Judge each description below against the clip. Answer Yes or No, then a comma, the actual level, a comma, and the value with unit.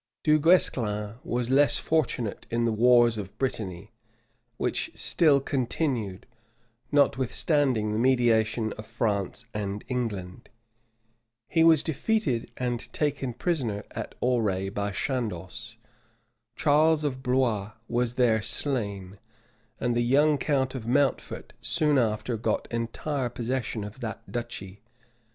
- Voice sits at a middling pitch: No, low, 120 Hz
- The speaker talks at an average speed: No, slow, 120 wpm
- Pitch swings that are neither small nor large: Yes, average, 4.2 semitones